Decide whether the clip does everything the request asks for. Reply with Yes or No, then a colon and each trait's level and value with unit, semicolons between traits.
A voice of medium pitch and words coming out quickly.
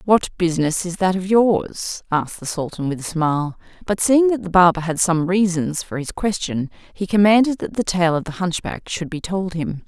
Yes: medium, 180 Hz; fast, 215 wpm